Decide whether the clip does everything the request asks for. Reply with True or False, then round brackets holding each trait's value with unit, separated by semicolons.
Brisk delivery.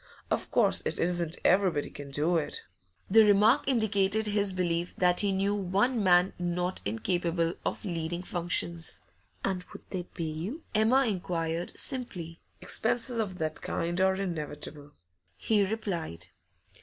False (140 wpm)